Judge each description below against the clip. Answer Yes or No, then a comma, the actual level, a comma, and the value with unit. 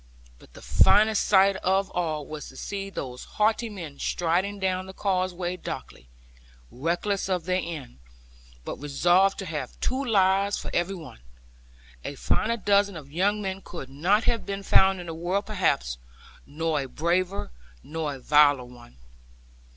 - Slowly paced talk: No, average, 160 wpm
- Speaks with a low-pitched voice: No, medium, 180 Hz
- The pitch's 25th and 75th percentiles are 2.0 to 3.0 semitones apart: No, average, 4.6 semitones